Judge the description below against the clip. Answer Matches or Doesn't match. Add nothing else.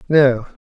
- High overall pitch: Doesn't match